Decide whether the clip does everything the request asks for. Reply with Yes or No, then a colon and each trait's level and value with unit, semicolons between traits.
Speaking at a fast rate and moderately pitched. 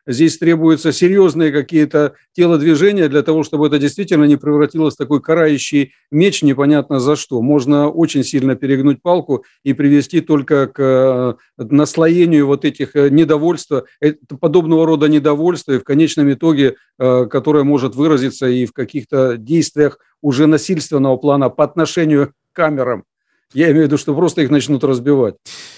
No: average, 145 wpm; medium, 150 Hz